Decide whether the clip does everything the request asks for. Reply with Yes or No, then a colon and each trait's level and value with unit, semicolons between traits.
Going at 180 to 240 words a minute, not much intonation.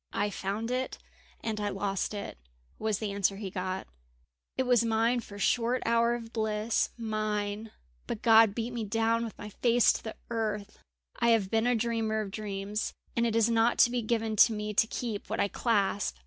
Yes: fast, 205 wpm; narrow, 2.0 semitones